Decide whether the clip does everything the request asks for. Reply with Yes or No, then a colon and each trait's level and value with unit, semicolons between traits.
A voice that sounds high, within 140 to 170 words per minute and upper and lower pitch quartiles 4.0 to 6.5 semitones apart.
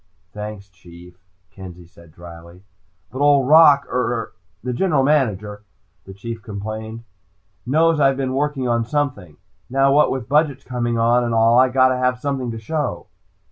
No: low, 120 Hz; average, 155 wpm; average, 4.7 semitones